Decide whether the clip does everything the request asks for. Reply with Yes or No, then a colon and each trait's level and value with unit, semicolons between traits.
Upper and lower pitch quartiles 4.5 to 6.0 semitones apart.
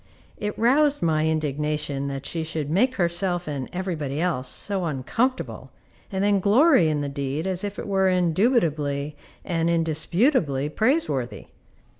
Yes: average, 5.3 semitones